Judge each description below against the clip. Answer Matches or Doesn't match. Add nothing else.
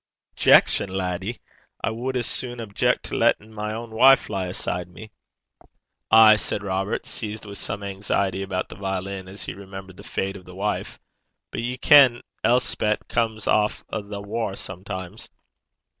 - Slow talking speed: Doesn't match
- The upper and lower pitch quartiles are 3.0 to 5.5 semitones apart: Doesn't match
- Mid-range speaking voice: Doesn't match